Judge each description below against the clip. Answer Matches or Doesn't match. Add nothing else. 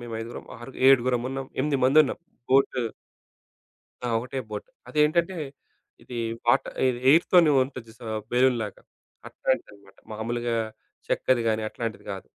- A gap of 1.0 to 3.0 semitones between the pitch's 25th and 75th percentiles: Matches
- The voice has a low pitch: Matches